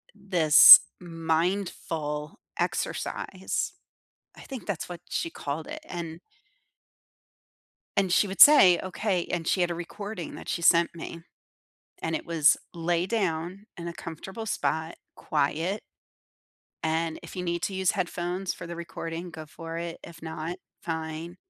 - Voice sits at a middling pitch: Yes, medium, 170 Hz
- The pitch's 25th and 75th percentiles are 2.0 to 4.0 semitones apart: Yes, narrow, 2.4 semitones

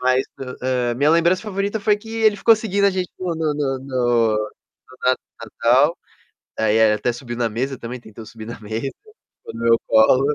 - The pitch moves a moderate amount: No, wide, 7.2 semitones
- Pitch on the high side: No, low, 130 Hz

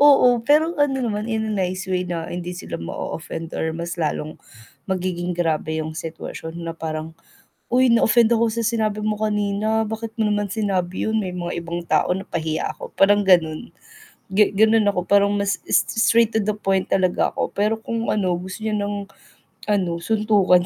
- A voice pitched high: Yes, high, 200 Hz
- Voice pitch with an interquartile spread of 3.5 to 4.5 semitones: Yes, average, 3.9 semitones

